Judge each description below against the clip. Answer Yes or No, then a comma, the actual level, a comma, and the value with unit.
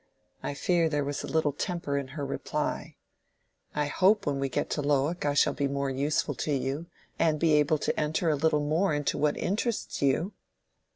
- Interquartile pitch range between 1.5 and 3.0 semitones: Yes, narrow, 2.4 semitones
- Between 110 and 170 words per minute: No, average, 195 wpm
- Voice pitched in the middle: Yes, medium, 150 Hz